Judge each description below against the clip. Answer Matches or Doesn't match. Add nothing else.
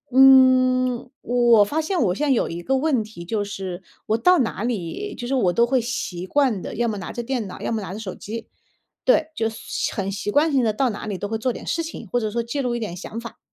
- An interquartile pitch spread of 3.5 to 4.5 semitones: Matches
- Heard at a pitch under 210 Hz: Doesn't match